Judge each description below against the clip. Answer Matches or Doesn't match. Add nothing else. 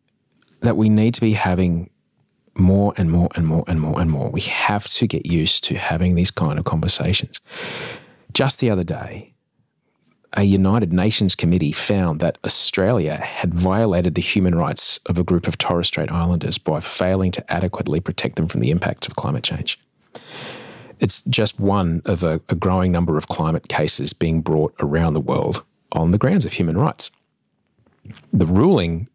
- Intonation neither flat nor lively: Matches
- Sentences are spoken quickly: Doesn't match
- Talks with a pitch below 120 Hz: Matches